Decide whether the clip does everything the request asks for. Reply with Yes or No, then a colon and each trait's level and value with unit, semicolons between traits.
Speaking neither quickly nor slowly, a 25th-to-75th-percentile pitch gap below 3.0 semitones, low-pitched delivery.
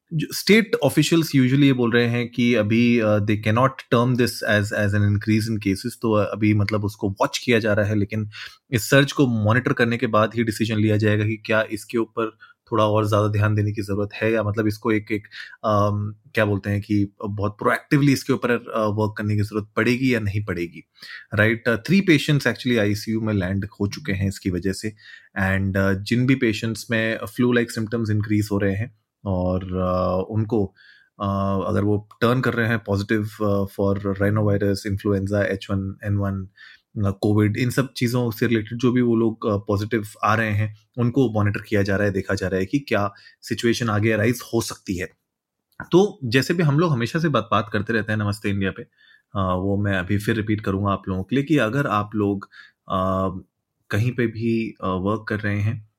No: fast, 200 wpm; narrow, 2.6 semitones; low, 105 Hz